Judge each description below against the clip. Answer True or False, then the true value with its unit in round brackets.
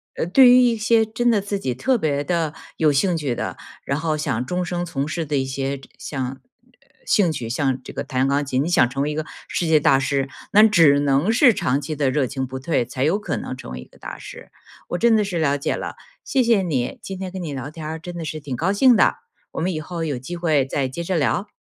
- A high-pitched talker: False (155 Hz)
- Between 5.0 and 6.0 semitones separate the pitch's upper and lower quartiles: True (5.4 semitones)